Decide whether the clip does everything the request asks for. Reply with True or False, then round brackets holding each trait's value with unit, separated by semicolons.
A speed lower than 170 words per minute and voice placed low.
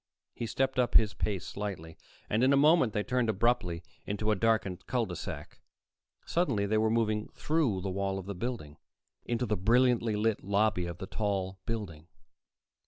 False (175 wpm; 105 Hz)